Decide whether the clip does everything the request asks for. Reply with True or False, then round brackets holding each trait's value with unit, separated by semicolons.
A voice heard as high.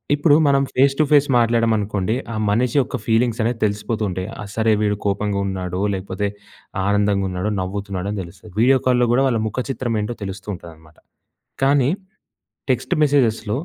False (105 Hz)